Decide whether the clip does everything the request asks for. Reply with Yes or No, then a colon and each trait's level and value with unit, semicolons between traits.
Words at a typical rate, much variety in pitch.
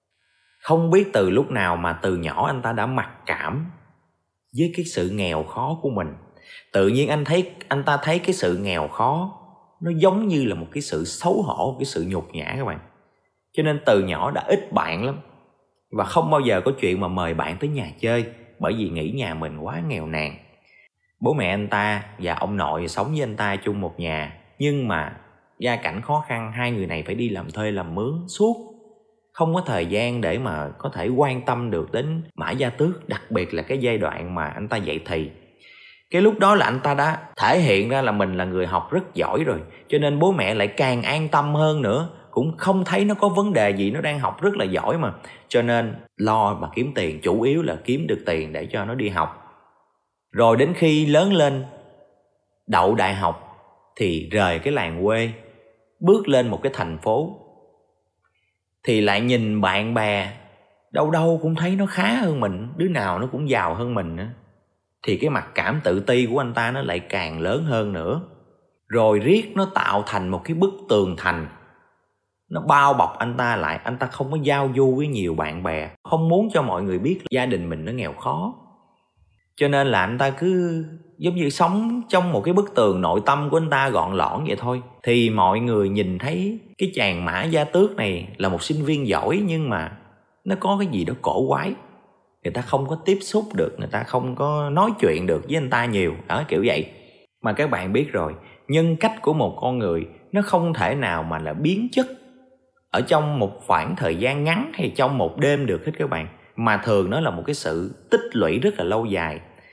Yes: average, 220 wpm; wide, 8.6 semitones